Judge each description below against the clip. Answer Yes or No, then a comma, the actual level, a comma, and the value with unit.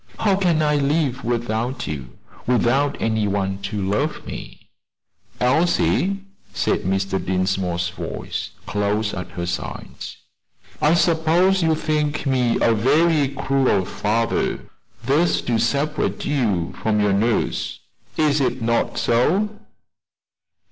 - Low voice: Yes, low, 125 Hz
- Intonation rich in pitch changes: Yes, wide, 6.7 semitones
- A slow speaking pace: Yes, slow, 120 wpm